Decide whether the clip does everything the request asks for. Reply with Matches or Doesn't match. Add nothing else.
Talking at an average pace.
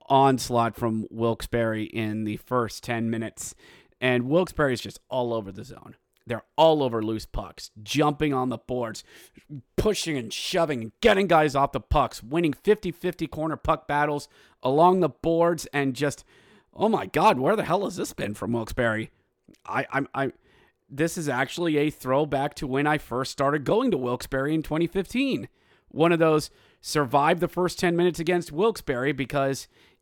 Matches